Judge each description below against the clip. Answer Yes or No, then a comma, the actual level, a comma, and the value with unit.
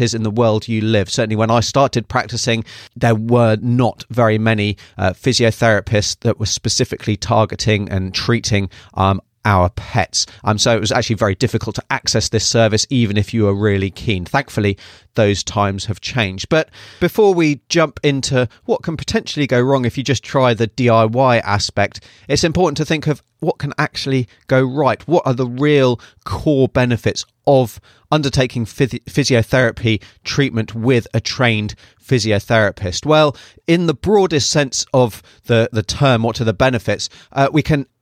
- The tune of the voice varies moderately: Yes, average, 3.8 semitones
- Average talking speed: Yes, average, 170 wpm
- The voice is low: Yes, low, 115 Hz